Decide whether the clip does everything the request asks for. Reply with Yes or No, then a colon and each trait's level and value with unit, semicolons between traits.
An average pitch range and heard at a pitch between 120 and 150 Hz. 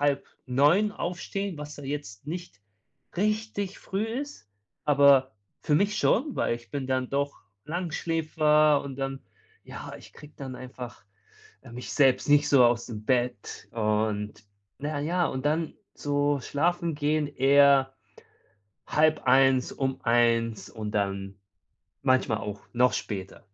Yes: average, 4.0 semitones; medium, 140 Hz